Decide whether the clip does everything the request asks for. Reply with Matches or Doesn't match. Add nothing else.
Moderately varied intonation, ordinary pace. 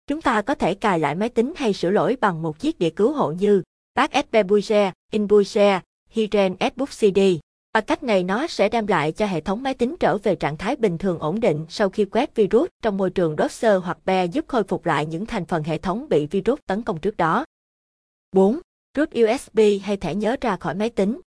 Matches